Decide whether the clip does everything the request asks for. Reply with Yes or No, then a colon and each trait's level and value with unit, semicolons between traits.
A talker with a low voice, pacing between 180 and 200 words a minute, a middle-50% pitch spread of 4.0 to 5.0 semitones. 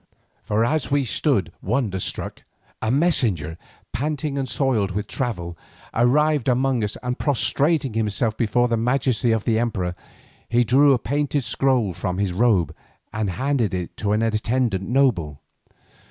No: low, 120 Hz; average, 150 wpm; average, 4.6 semitones